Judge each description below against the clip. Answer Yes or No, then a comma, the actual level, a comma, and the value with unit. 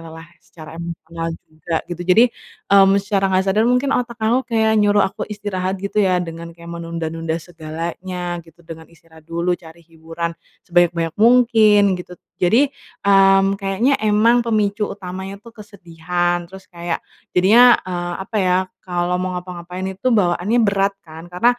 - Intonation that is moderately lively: Yes, average, 3.5 semitones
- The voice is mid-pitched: Yes, medium, 180 Hz